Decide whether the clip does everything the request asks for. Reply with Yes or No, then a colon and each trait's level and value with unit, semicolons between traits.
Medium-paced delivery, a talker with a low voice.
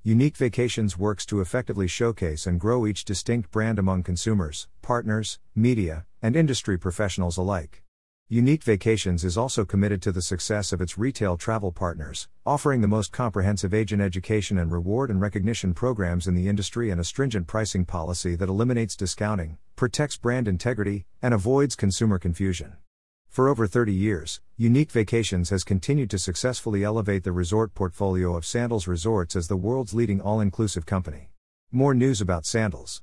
Yes: average, 160 wpm; low, 100 Hz